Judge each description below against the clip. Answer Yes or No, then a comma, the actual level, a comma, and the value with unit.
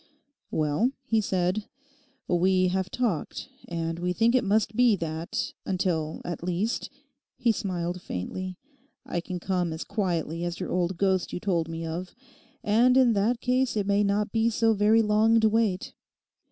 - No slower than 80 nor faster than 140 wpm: No, average, 165 wpm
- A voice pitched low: No, high, 190 Hz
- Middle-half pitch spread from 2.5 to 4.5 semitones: Yes, average, 4.1 semitones